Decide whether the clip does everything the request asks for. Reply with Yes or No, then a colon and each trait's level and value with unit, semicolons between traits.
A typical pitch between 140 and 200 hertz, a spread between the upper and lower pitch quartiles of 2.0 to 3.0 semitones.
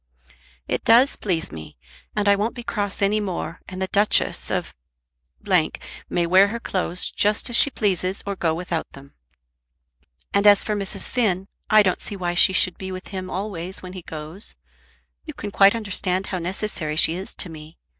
Yes: high, 190 Hz; average, 2.7 semitones